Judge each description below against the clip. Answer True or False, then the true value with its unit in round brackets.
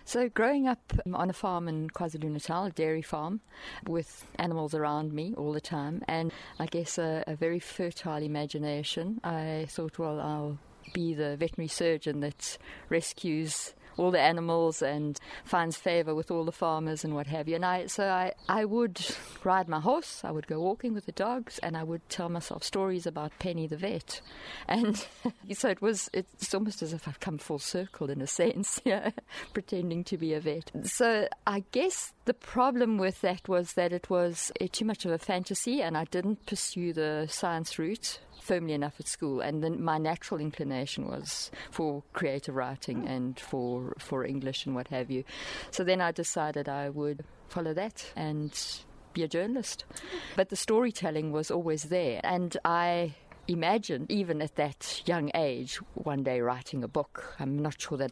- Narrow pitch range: False (3.7 semitones)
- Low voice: False (165 Hz)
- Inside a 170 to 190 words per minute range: True (185 wpm)